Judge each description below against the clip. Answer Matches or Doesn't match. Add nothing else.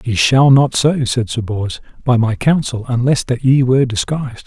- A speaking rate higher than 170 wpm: Matches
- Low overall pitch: Matches